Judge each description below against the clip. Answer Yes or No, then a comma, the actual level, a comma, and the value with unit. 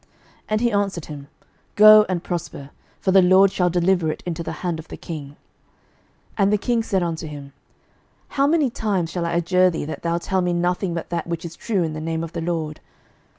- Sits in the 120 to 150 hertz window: No, medium, 175 Hz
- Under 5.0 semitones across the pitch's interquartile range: Yes, average, 2.9 semitones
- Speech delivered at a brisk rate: Yes, fast, 220 wpm